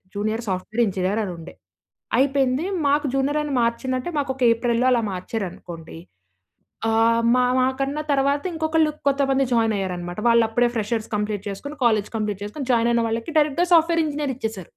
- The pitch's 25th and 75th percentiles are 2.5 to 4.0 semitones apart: No, average, 4.7 semitones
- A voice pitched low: No, high, 235 Hz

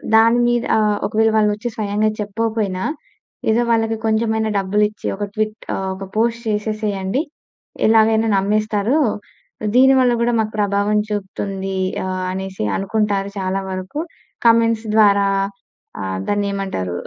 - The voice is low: No, high, 210 Hz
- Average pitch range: No, narrow, 2.2 semitones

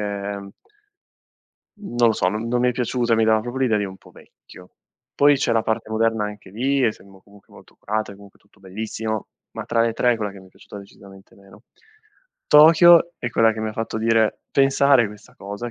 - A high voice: No, low, 110 Hz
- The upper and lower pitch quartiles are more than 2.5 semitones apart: Yes, average, 2.9 semitones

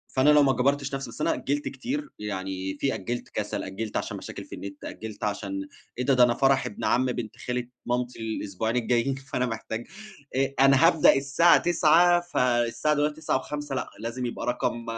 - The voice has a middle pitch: No, low, 125 Hz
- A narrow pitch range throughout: No, average, 3.7 semitones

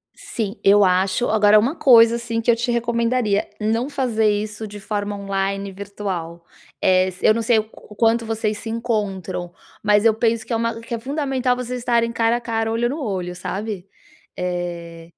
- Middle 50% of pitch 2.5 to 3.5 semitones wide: Yes, average, 2.8 semitones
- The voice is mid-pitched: No, high, 220 Hz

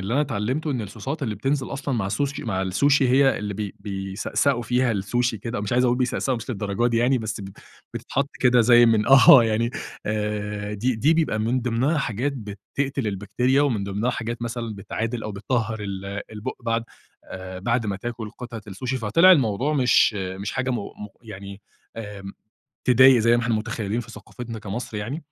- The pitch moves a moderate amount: Yes, average, 3.6 semitones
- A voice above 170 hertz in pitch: No, low, 115 Hz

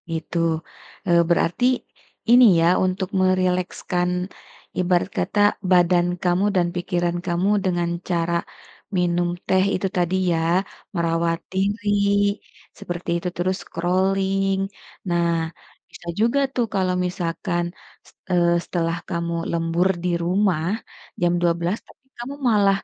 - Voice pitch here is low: No, medium, 180 Hz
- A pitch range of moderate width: No, narrow, 1.6 semitones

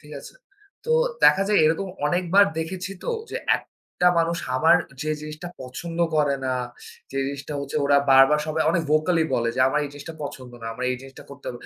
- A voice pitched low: No, medium, 155 Hz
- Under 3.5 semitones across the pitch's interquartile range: No, average, 3.8 semitones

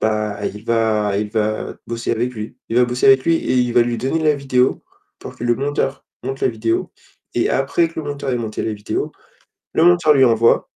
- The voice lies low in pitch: Yes, low, 120 Hz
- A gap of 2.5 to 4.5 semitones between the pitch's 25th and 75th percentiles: Yes, average, 3.5 semitones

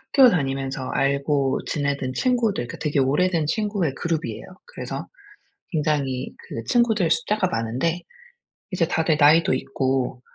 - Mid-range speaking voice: Yes, medium, 150 Hz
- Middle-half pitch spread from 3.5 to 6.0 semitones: Yes, average, 5.2 semitones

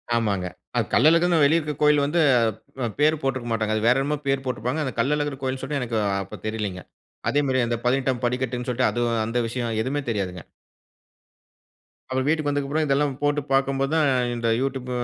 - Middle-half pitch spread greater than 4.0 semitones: No, average, 3.5 semitones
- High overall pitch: No, low, 130 Hz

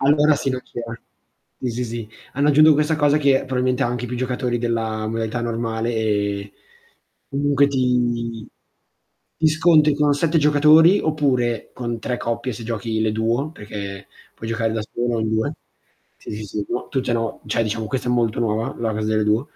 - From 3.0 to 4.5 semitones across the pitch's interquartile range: Yes, average, 3.9 semitones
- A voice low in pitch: Yes, low, 120 Hz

